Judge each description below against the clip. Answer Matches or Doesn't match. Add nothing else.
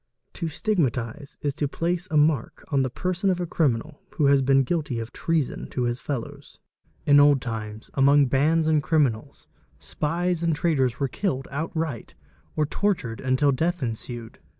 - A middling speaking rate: Matches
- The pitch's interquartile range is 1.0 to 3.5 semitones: Doesn't match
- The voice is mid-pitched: Matches